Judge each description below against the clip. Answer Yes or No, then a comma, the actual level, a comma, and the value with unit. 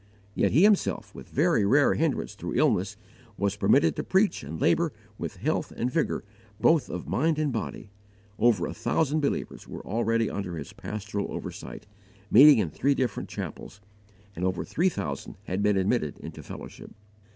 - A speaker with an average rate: Yes, average, 165 wpm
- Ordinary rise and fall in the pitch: No, wide, 7.2 semitones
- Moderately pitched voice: No, low, 115 Hz